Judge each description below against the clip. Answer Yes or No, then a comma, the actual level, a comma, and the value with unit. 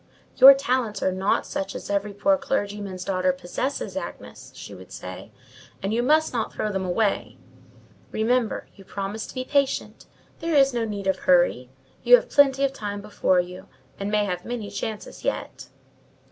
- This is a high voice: Yes, high, 210 Hz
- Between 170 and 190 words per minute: Yes, average, 175 wpm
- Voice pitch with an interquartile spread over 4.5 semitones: Yes, average, 5.0 semitones